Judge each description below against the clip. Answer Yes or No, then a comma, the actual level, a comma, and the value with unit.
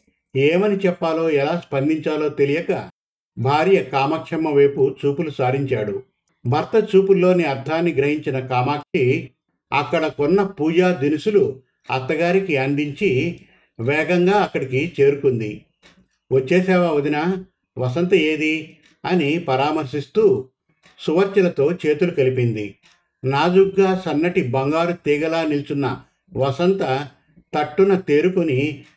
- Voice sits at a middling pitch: Yes, medium, 155 Hz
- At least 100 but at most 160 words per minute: No, average, 85 wpm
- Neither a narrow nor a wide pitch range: Yes, average, 4.3 semitones